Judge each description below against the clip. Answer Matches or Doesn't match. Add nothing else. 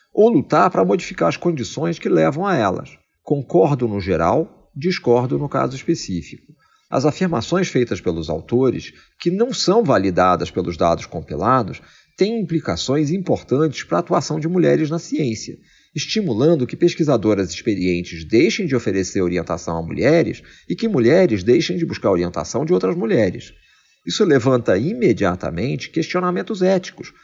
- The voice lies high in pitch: Doesn't match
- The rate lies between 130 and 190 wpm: Matches